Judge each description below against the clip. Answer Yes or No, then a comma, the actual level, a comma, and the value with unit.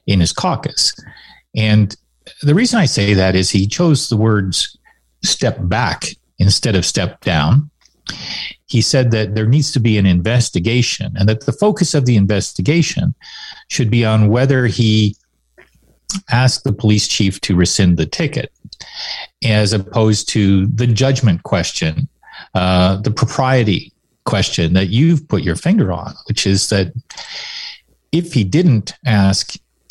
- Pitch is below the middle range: Yes, low, 110 Hz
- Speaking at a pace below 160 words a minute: Yes, average, 145 wpm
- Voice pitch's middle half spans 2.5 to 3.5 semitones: No, average, 5.1 semitones